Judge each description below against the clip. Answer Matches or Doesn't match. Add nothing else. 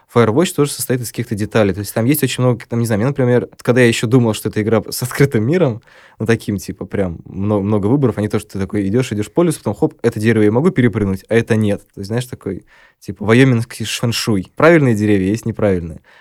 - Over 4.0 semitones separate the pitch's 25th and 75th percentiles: Doesn't match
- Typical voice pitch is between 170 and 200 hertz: Doesn't match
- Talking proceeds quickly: Matches